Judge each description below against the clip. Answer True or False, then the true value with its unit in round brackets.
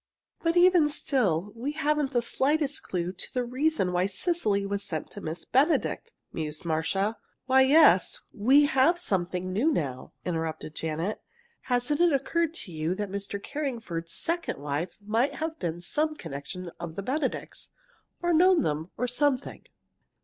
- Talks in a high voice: True (230 Hz)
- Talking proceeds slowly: False (155 wpm)